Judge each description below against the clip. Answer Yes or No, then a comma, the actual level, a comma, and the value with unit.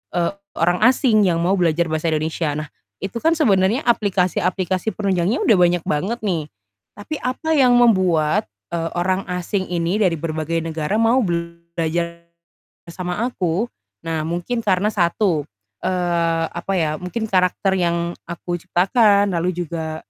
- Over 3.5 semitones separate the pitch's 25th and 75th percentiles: No, average, 3.2 semitones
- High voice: No, medium, 180 Hz